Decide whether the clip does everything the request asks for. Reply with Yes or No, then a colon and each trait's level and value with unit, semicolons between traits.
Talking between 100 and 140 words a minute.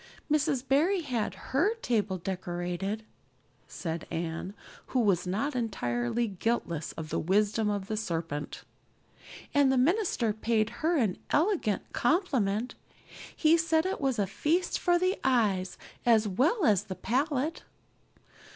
Yes: slow, 135 wpm